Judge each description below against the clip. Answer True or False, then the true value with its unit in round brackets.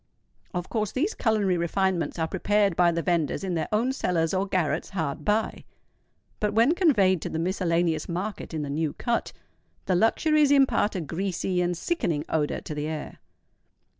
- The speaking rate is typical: True (170 wpm)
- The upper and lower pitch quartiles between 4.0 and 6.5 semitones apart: True (4.4 semitones)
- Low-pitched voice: False (185 Hz)